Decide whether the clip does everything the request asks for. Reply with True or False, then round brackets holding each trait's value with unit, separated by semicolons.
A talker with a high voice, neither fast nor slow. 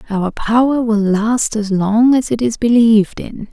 True (225 Hz; 190 wpm)